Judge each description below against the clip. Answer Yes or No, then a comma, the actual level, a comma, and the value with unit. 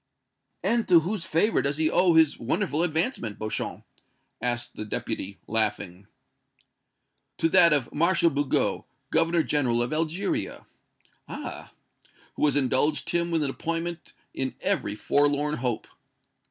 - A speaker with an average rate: No, slow, 130 wpm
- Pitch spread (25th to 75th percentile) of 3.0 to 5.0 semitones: No, wide, 5.5 semitones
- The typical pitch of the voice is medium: Yes, medium, 150 Hz